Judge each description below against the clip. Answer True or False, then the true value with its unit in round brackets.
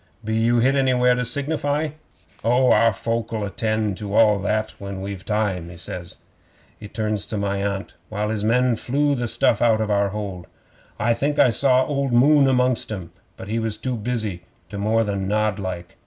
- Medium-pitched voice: False (110 Hz)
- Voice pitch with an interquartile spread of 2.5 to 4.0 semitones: True (3.6 semitones)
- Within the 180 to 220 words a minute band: True (200 wpm)